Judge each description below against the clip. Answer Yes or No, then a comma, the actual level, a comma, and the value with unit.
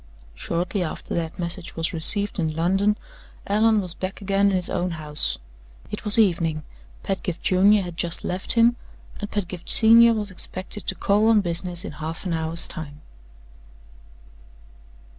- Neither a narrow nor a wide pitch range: Yes, average, 3.6 semitones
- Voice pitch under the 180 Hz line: No, medium, 185 Hz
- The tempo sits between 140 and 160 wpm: Yes, average, 155 wpm